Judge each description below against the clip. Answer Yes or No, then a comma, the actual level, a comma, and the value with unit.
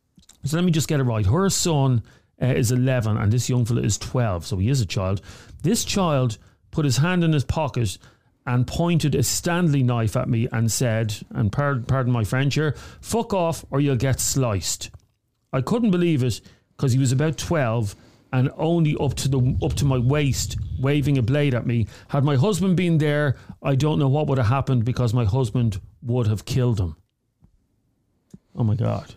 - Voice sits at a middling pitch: No, low, 125 Hz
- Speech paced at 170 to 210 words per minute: Yes, average, 200 wpm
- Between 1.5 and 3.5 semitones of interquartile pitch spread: No, average, 4.1 semitones